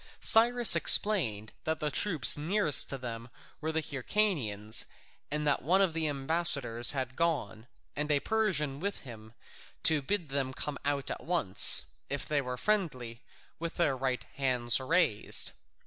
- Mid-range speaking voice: Yes, medium, 145 Hz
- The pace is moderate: Yes, average, 150 wpm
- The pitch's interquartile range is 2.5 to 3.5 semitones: No, average, 5.0 semitones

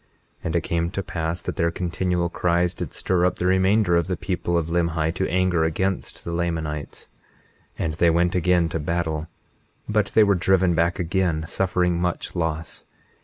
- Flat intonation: Yes, narrow, 1.7 semitones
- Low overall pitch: Yes, very low, 85 Hz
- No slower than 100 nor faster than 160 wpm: No, average, 180 wpm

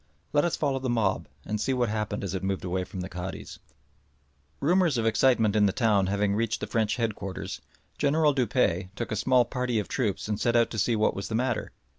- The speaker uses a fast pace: Yes, fast, 220 wpm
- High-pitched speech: No, low, 110 Hz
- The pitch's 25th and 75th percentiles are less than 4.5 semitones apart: Yes, average, 4.0 semitones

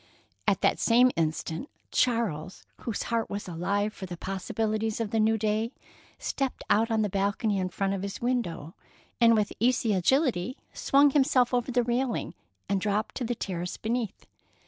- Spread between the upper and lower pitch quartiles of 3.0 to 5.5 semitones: Yes, average, 3.7 semitones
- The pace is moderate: Yes, average, 170 wpm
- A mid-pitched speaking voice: No, high, 220 Hz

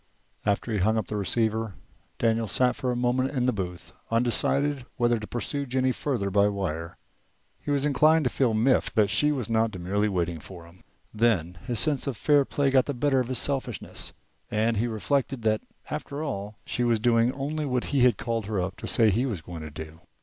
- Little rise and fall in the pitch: No, average, 4.4 semitones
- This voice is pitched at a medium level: No, low, 115 Hz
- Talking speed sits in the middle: No, fast, 215 wpm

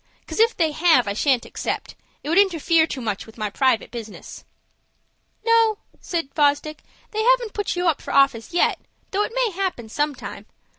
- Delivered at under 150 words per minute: No, average, 180 wpm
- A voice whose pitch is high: Yes, very high, 320 Hz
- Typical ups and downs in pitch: No, wide, 7.3 semitones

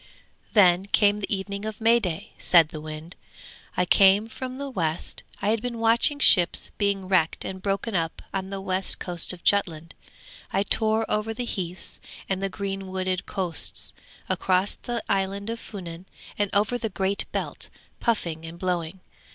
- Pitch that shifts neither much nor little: Yes, average, 3.0 semitones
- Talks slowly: No, average, 170 wpm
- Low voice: No, high, 195 Hz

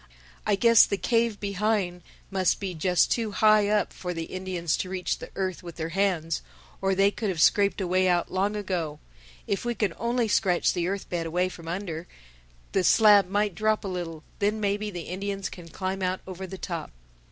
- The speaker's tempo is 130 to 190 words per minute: No, average, 200 wpm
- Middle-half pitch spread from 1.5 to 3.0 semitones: Yes, narrow, 2.6 semitones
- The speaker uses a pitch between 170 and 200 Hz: Yes, high, 190 Hz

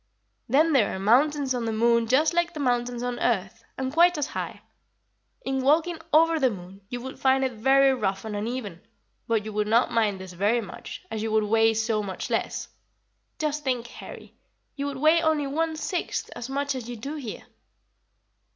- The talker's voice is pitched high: Yes, very high, 250 Hz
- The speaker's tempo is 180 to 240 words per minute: Yes, average, 195 wpm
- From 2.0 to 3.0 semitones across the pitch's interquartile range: No, average, 4.6 semitones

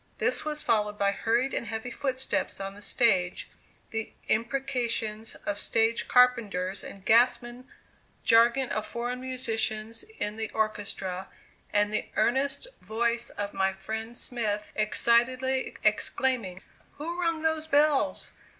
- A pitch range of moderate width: Yes, average, 3.4 semitones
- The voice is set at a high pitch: Yes, high, 230 Hz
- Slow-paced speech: Yes, slow, 125 wpm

